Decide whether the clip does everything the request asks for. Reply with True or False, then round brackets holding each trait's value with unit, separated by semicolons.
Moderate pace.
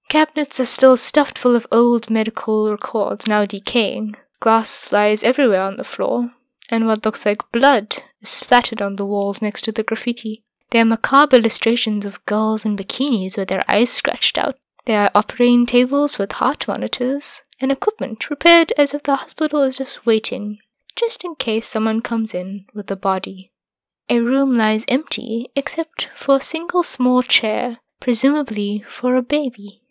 True (170 wpm)